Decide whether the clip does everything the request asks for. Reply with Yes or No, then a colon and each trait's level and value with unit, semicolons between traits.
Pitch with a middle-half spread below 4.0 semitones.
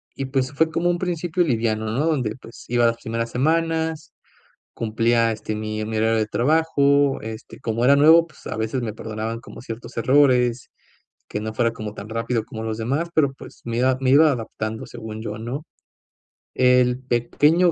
No: average, 4.4 semitones